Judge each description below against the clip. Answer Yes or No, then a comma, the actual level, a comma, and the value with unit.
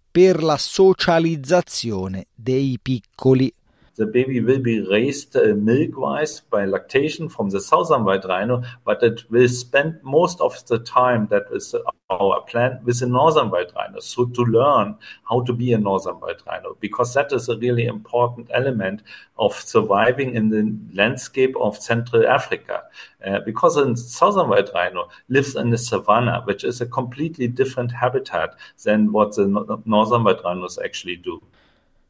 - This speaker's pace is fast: No, average, 160 wpm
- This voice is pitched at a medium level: No, low, 125 Hz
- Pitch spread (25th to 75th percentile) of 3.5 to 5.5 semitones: No, average, 2.7 semitones